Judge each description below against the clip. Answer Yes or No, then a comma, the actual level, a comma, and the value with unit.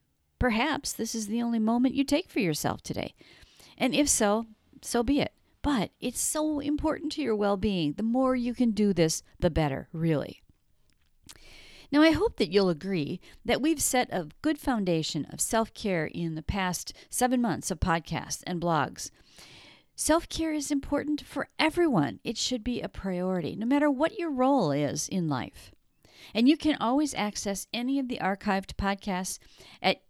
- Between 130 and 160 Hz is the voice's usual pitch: No, high, 225 Hz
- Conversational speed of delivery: Yes, average, 175 wpm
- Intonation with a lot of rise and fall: Yes, wide, 8.0 semitones